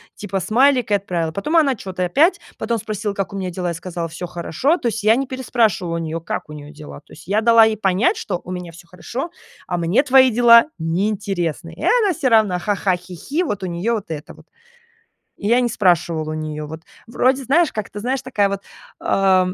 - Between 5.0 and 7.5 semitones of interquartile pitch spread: Yes, wide, 5.4 semitones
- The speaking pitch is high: Yes, high, 200 Hz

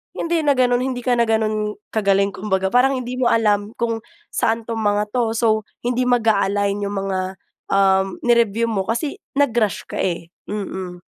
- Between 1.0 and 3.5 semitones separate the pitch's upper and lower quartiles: Yes, average, 3.2 semitones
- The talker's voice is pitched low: No, high, 220 Hz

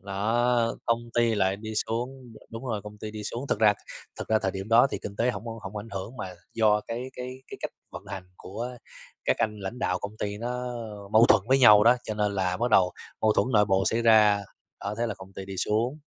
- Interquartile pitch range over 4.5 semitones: No, narrow, 2.6 semitones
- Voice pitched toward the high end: No, low, 110 Hz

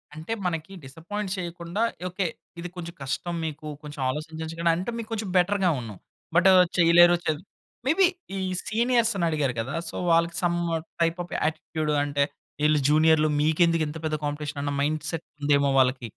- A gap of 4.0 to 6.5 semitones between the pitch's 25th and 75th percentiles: No, average, 2.8 semitones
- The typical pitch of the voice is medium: Yes, medium, 160 Hz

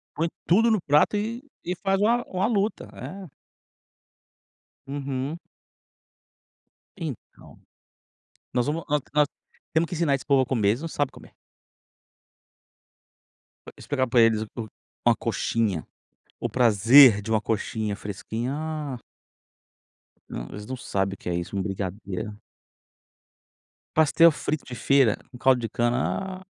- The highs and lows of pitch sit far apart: Yes, wide, 6.8 semitones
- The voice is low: Yes, low, 130 Hz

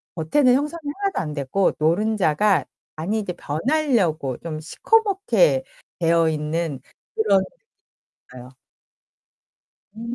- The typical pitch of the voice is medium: Yes, medium, 180 Hz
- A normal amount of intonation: No, wide, 8.1 semitones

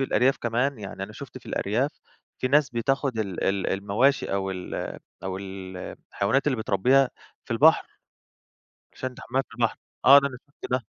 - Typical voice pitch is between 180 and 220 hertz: No, low, 120 Hz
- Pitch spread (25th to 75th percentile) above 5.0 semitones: Yes, wide, 5.4 semitones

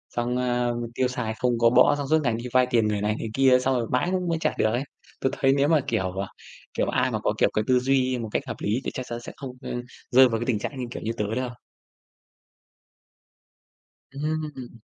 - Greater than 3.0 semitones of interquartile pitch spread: No, narrow, 2.6 semitones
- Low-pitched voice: Yes, low, 125 Hz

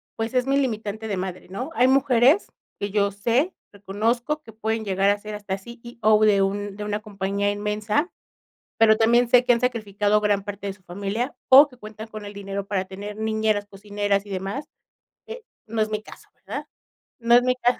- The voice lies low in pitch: No, high, 215 Hz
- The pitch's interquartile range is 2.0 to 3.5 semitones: Yes, average, 2.8 semitones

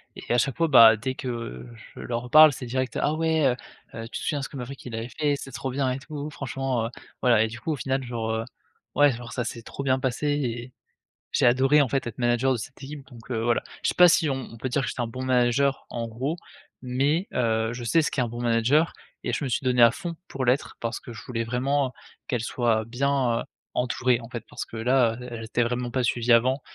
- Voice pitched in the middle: No, low, 125 Hz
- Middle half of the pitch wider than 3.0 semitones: No, average, 2.7 semitones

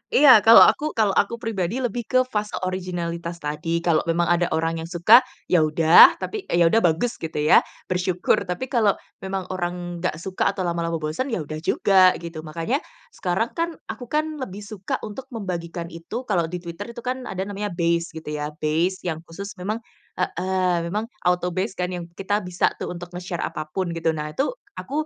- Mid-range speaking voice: Yes, medium, 180 Hz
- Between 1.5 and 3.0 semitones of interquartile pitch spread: No, average, 3.4 semitones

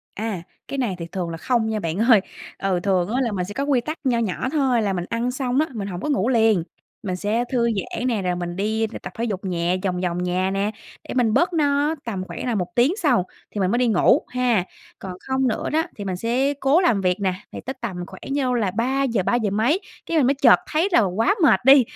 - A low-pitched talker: No, high, 225 Hz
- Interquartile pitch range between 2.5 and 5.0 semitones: No, wide, 5.5 semitones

